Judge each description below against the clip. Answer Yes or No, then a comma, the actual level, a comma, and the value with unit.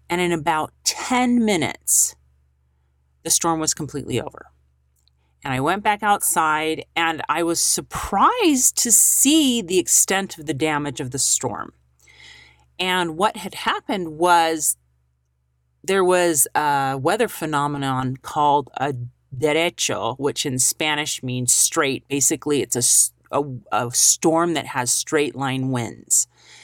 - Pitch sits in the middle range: Yes, medium, 145 Hz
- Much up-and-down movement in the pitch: Yes, wide, 6.5 semitones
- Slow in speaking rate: Yes, slow, 130 wpm